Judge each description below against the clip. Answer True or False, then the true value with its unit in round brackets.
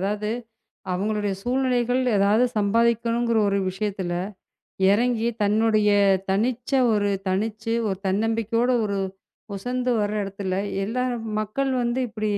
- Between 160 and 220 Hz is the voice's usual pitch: True (215 Hz)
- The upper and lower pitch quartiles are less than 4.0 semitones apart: True (2.8 semitones)